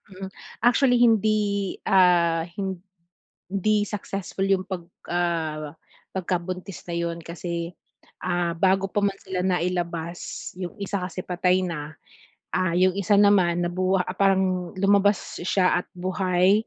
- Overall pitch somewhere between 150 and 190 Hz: Yes, medium, 185 Hz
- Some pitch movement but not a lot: No, narrow, 2.1 semitones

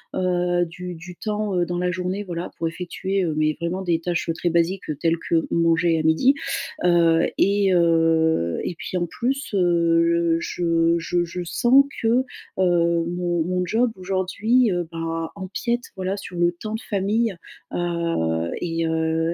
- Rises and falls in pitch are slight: Yes, narrow, 2.1 semitones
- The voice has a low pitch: No, medium, 175 Hz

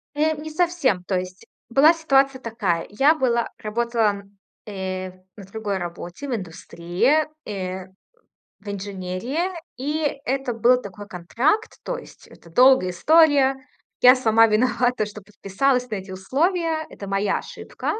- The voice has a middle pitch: No, high, 230 Hz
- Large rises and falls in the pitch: Yes, wide, 6.2 semitones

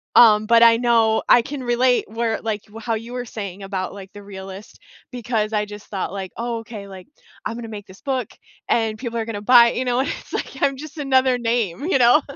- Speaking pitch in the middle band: No, high, 230 Hz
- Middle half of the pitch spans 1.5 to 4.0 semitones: Yes, average, 2.8 semitones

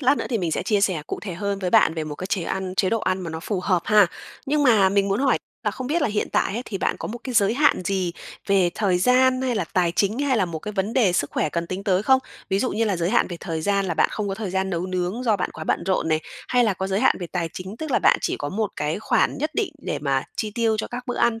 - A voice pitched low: No, high, 195 Hz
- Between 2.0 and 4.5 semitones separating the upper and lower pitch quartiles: Yes, average, 4.2 semitones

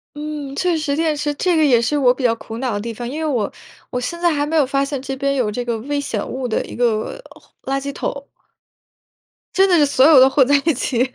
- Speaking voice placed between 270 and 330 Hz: Yes, very high, 275 Hz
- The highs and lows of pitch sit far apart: No, average, 3.3 semitones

